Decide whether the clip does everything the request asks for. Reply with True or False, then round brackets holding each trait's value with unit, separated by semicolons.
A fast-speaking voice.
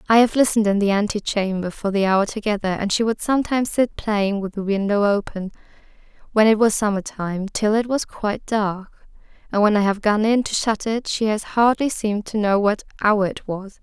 True (215 wpm)